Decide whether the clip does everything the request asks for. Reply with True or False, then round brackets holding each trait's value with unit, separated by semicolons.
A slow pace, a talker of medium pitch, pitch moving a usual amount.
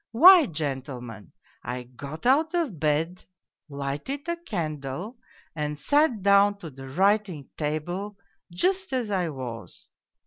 False (125 wpm; 170 Hz; 8.4 semitones)